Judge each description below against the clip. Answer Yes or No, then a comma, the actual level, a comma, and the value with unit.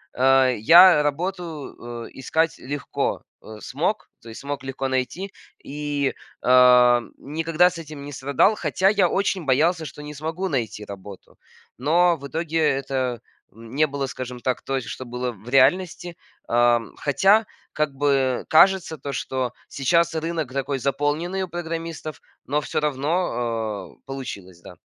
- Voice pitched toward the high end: No, medium, 140 Hz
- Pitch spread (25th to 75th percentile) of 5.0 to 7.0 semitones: No, average, 4.4 semitones